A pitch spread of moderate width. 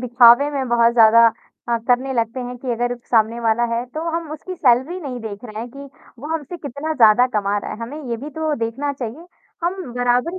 Yes: average, 3.6 semitones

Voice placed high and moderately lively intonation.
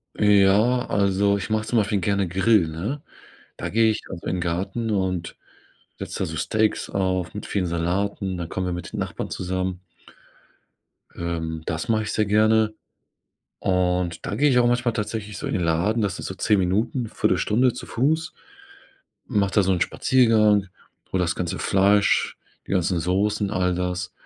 No: low, 100 Hz; average, 3.1 semitones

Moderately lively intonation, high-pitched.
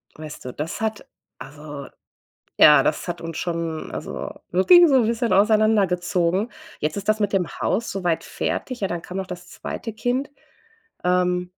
No: average, 4.4 semitones; medium, 180 Hz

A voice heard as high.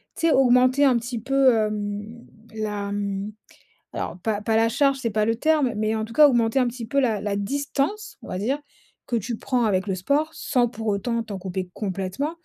Yes: high, 225 Hz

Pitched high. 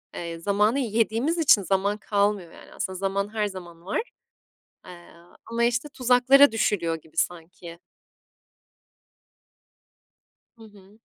Yes: high, 205 Hz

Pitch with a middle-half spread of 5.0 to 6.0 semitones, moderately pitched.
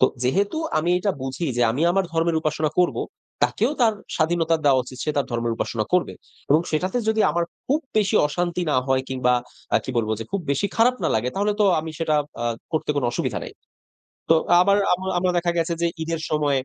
Yes: average, 5.3 semitones; medium, 165 Hz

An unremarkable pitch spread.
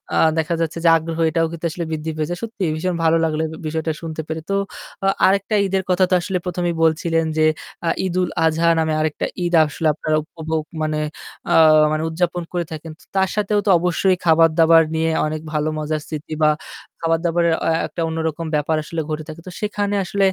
No: narrow, 2.0 semitones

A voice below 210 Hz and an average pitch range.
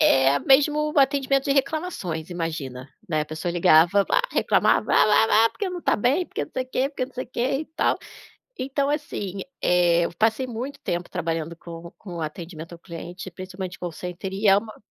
No: high, 190 Hz; wide, 7.9 semitones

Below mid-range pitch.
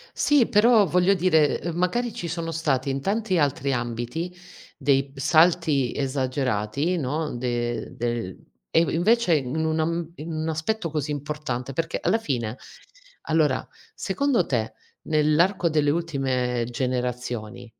No: medium, 150 Hz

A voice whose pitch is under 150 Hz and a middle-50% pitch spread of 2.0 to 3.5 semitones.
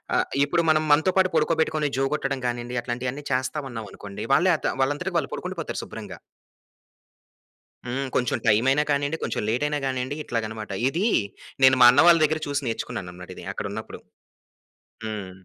No: low, 135 Hz; average, 4.0 semitones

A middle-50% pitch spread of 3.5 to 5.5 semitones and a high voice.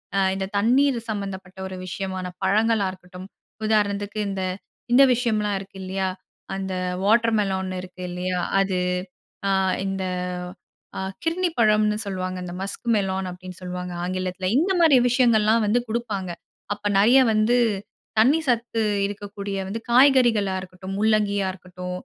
No: average, 3.1 semitones; high, 200 Hz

